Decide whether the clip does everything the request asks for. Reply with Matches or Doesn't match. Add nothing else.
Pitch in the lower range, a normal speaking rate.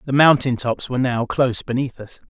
Doesn't match